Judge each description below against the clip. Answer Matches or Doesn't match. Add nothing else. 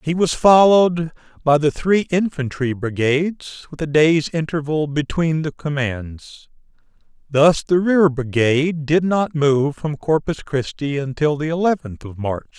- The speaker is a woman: Doesn't match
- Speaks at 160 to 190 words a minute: Doesn't match